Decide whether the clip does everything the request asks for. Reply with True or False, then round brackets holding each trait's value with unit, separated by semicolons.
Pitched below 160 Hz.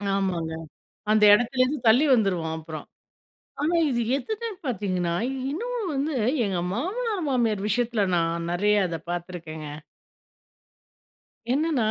False (215 Hz)